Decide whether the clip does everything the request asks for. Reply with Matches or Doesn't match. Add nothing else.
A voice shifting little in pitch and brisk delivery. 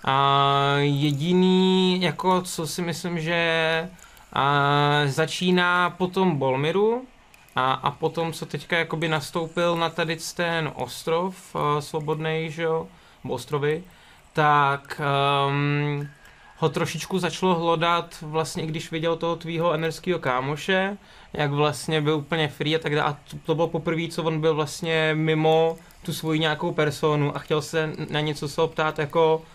Doesn't match